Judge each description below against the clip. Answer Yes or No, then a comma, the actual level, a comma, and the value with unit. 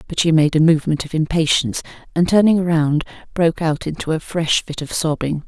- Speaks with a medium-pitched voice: Yes, medium, 160 Hz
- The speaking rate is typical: Yes, average, 195 wpm